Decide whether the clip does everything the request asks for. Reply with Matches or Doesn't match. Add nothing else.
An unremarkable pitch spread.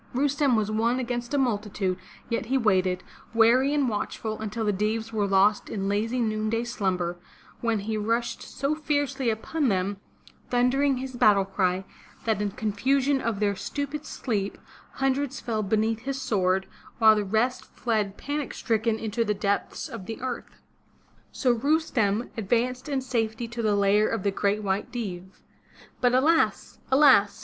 Matches